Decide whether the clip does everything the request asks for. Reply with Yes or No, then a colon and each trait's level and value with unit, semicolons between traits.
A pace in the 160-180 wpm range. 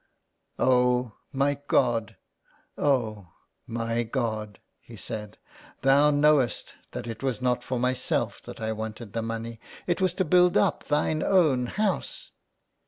No: average, 140 wpm